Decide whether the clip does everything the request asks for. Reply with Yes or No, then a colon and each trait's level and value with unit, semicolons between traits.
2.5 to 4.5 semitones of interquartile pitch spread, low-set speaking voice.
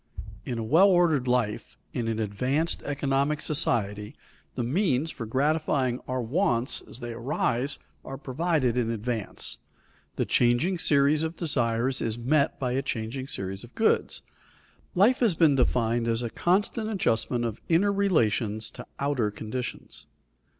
No: average, 5.0 semitones; low, 130 Hz